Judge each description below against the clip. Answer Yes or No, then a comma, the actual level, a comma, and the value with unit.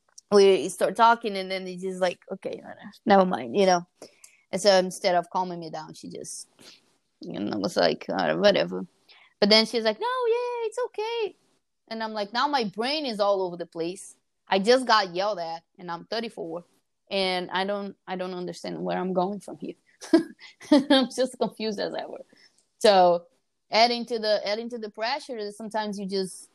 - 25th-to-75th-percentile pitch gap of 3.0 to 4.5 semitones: Yes, average, 4.1 semitones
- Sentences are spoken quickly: No, average, 195 wpm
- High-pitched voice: Yes, high, 205 Hz